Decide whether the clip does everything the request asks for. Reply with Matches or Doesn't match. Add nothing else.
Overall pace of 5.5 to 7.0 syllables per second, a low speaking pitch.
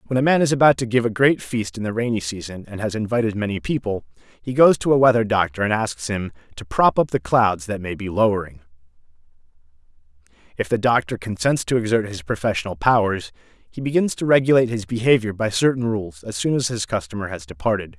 Matches